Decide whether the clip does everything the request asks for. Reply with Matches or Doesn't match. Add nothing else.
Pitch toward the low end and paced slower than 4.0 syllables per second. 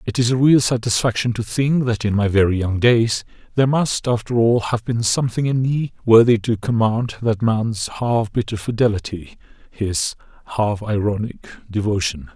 Doesn't match